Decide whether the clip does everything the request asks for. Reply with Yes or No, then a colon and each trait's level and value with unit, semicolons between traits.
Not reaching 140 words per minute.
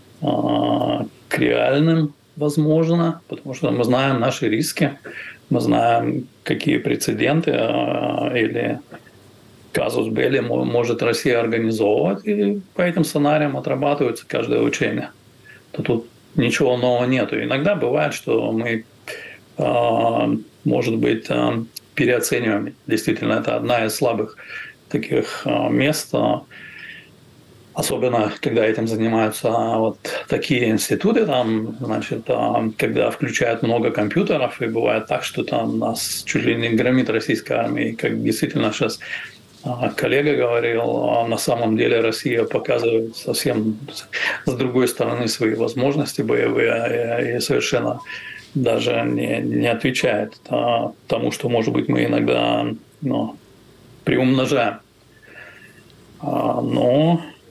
Yes: slow, 110 wpm